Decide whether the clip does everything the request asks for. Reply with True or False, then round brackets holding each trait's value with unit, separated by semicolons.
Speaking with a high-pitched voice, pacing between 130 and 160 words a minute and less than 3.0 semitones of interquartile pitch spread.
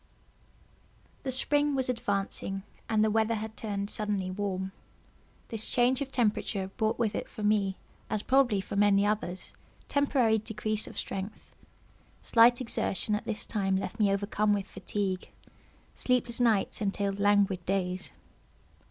True (210 Hz; 135 wpm; 2.5 semitones)